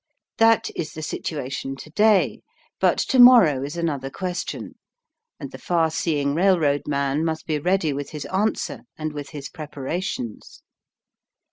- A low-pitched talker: No, medium, 155 Hz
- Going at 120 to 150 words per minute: Yes, average, 145 wpm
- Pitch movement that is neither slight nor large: Yes, average, 4.0 semitones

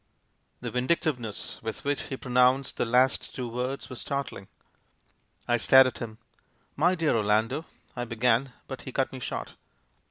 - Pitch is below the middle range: Yes, low, 125 Hz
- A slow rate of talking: No, average, 160 wpm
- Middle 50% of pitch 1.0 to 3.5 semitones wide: Yes, narrow, 2.5 semitones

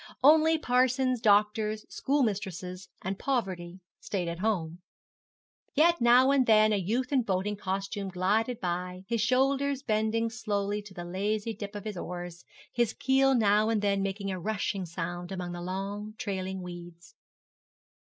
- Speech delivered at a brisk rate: No, average, 145 wpm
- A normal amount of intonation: Yes, average, 4.1 semitones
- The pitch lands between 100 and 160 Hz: No, high, 205 Hz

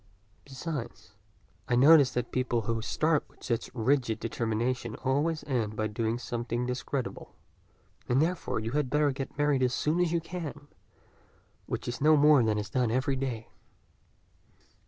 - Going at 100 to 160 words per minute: Yes, average, 155 wpm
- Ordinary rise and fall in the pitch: Yes, average, 4.0 semitones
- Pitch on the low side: Yes, low, 130 Hz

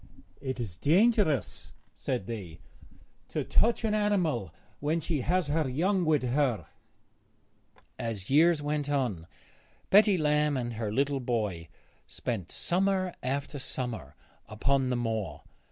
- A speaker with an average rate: No, slow, 125 wpm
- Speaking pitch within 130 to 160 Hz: Yes, medium, 140 Hz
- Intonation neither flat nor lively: No, wide, 6.0 semitones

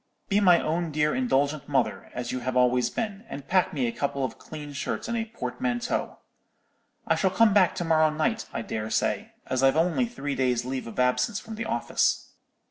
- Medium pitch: Yes, medium, 155 Hz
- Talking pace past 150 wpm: Yes, fast, 205 wpm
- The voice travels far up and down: Yes, wide, 7.9 semitones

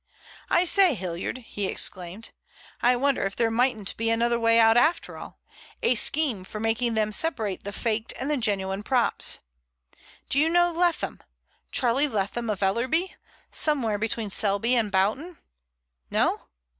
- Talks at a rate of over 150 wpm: No, average, 145 wpm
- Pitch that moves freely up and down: No, average, 4.6 semitones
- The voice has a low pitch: No, high, 230 Hz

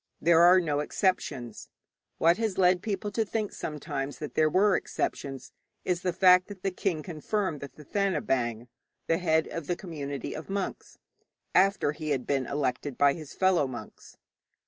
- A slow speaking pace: No, average, 165 wpm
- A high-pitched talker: No, medium, 165 Hz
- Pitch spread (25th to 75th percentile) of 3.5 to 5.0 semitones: Yes, average, 4.6 semitones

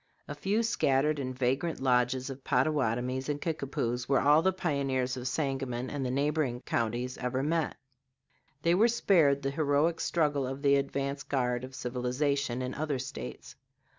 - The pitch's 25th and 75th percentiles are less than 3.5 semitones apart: Yes, average, 2.7 semitones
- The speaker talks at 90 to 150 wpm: No, average, 160 wpm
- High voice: No, low, 135 Hz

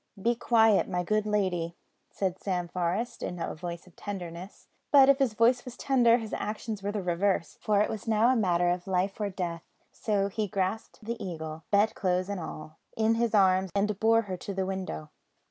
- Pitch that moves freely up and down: No, average, 3.6 semitones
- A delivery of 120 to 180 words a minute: No, average, 195 wpm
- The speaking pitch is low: No, high, 200 Hz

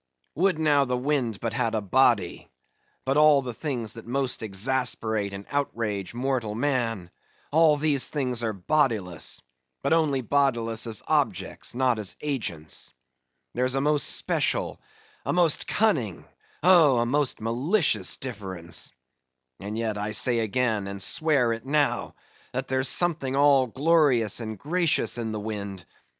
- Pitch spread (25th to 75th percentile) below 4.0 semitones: No, average, 4.8 semitones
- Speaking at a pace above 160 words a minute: No, average, 145 wpm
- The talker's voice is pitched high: No, low, 125 Hz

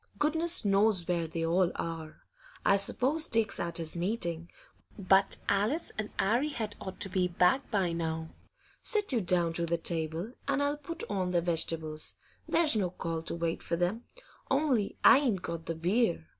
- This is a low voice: No, medium, 185 Hz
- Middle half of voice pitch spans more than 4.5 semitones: Yes, wide, 5.6 semitones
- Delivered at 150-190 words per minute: Yes, average, 175 wpm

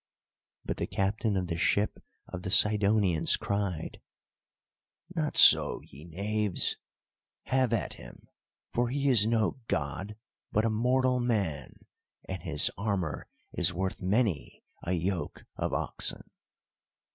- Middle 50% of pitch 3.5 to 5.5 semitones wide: Yes, average, 4.1 semitones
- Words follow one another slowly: Yes, slow, 125 wpm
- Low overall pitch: Yes, low, 100 Hz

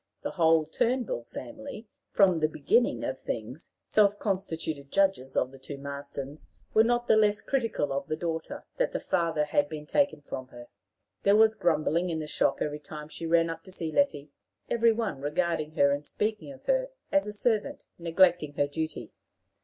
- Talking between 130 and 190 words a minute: Yes, average, 185 wpm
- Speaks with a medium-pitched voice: Yes, medium, 165 Hz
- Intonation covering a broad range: Yes, wide, 6.2 semitones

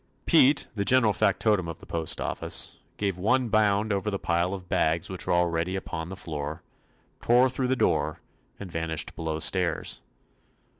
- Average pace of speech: Yes, average, 160 wpm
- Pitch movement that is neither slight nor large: Yes, average, 4.4 semitones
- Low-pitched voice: Yes, very low, 95 Hz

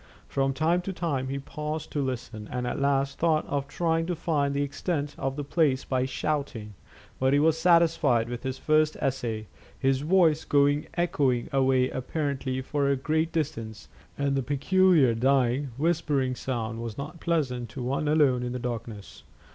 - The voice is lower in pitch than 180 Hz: Yes, medium, 140 Hz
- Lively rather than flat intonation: No, average, 3.3 semitones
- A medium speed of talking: Yes, average, 170 wpm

